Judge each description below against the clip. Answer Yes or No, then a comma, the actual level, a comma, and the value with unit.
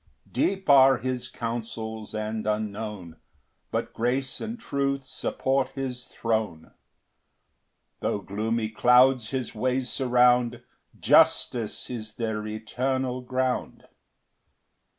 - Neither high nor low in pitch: No, low, 120 Hz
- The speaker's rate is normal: No, slow, 100 wpm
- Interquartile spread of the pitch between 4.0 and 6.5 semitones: No, average, 3.0 semitones